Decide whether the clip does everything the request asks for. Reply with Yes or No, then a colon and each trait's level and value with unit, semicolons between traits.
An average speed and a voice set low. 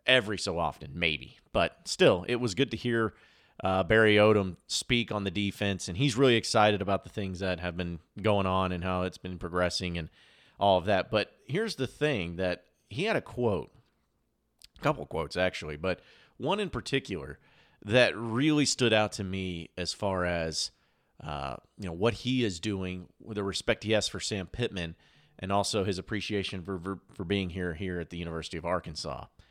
Yes: average, 195 wpm; very low, 95 Hz